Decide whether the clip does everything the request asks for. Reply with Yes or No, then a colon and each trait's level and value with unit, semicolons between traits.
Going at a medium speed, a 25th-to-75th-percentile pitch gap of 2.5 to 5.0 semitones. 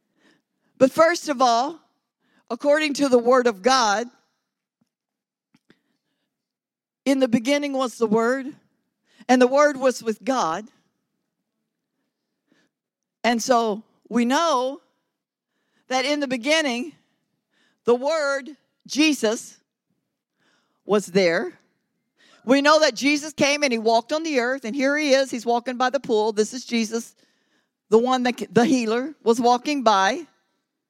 No: slow, 130 wpm; average, 3.6 semitones